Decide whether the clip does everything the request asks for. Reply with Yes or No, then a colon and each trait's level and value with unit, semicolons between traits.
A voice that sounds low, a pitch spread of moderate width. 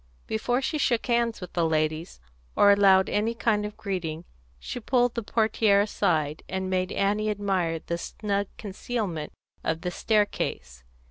No: high, 200 Hz; average, 4.3 semitones